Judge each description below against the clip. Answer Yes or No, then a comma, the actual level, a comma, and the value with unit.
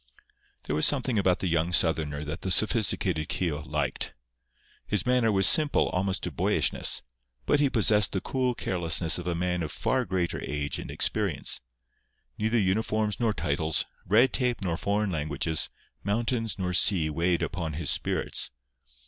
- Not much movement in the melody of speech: No, average, 5.0 semitones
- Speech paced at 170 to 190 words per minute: No, average, 155 wpm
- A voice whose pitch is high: No, very low, 95 Hz